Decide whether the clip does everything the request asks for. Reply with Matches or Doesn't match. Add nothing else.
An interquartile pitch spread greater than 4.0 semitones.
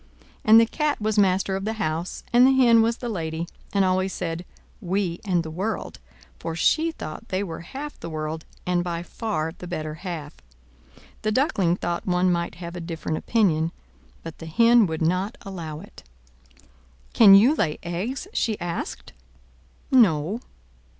Matches